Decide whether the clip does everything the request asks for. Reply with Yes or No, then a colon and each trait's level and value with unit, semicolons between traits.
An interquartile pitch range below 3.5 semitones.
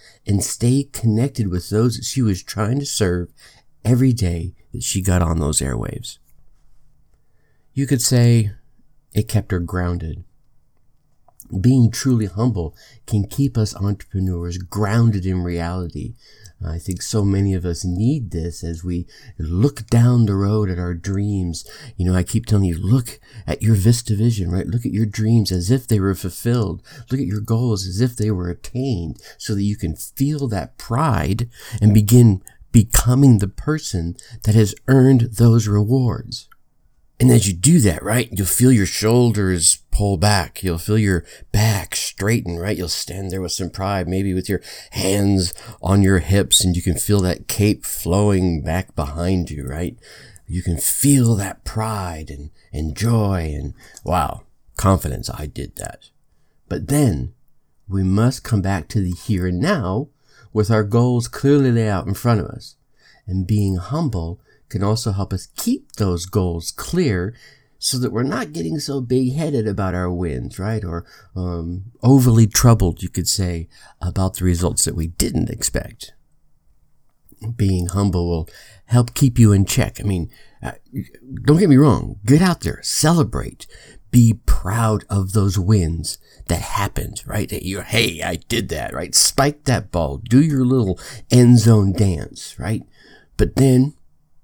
No: average, 4.8 semitones